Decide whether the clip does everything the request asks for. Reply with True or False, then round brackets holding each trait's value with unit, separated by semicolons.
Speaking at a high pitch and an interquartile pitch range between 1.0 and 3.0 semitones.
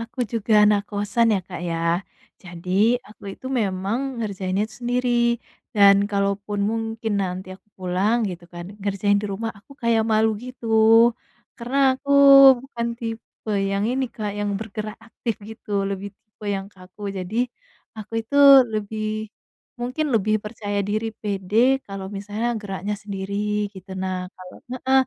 True (210 Hz; 2.5 semitones)